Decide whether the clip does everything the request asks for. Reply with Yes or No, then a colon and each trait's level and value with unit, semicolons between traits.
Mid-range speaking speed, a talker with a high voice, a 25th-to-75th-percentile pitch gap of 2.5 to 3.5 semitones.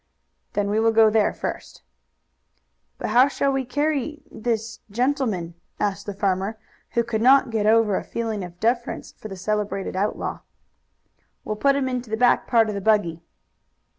Yes: average, 165 wpm; high, 220 Hz; average, 3.0 semitones